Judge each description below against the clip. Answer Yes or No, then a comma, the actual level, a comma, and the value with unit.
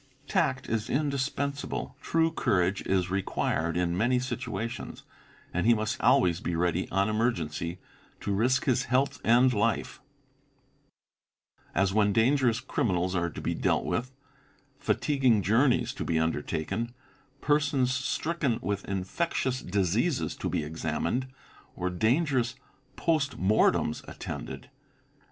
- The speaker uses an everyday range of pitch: No, wide, 5.9 semitones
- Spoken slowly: Yes, slow, 125 wpm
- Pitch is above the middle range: No, low, 115 Hz